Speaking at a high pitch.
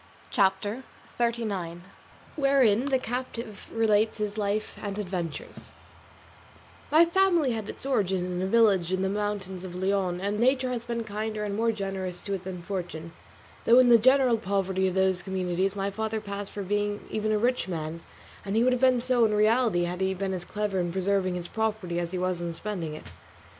Yes: high, 205 Hz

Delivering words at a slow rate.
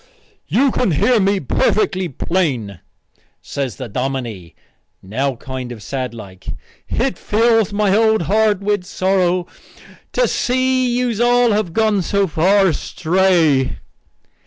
Yes: slow, 130 wpm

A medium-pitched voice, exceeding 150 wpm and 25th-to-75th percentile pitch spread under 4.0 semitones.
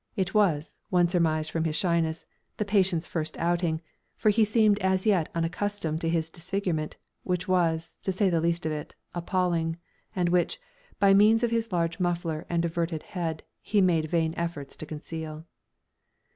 Yes: medium, 170 Hz; average, 170 wpm; average, 2.7 semitones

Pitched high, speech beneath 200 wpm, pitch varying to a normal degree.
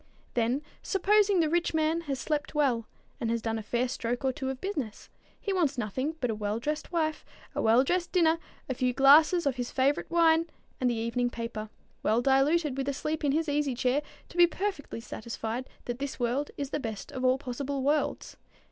No: very high, 275 Hz; fast, 205 wpm; average, 4.5 semitones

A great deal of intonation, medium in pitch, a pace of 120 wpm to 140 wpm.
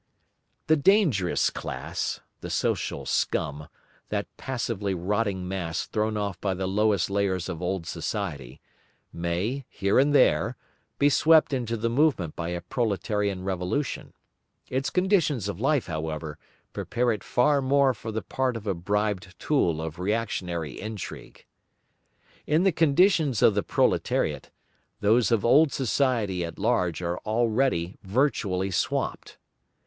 No: wide, 6.3 semitones; low, 105 Hz; slow, 135 wpm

